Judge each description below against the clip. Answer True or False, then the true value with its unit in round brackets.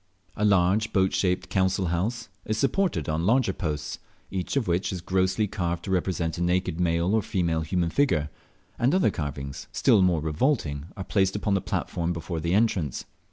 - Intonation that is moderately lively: True (3.4 semitones)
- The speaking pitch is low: True (90 Hz)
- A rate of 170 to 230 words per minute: True (180 wpm)